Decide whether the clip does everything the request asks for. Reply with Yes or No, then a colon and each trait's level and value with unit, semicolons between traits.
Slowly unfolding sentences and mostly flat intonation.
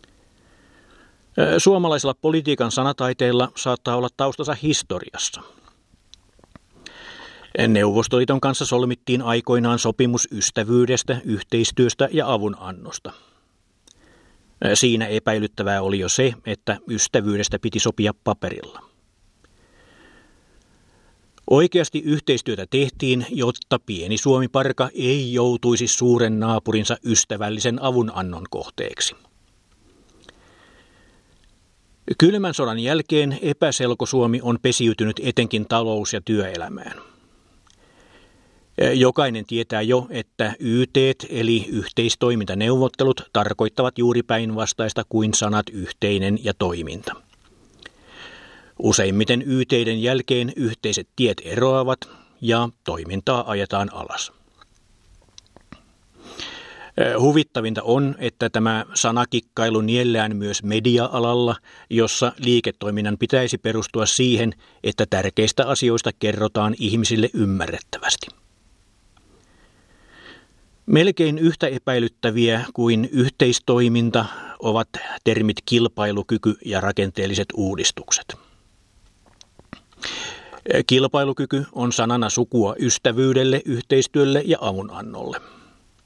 No: slow, 80 wpm; average, 3.3 semitones